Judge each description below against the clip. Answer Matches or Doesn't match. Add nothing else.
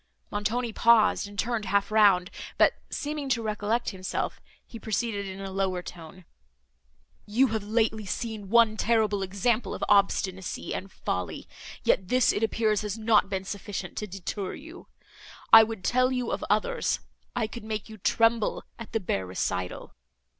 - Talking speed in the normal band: Matches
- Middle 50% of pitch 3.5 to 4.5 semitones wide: Doesn't match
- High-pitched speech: Matches